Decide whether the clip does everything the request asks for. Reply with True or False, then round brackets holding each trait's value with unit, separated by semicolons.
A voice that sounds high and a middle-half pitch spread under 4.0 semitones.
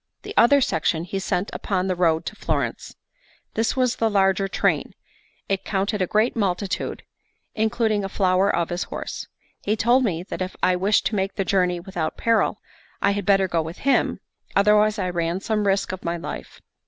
True (195 Hz; 2.7 semitones)